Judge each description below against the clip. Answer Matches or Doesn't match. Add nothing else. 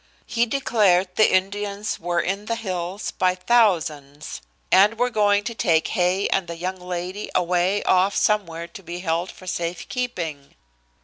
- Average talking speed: Matches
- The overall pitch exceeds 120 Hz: Matches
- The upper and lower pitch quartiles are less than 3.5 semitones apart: Matches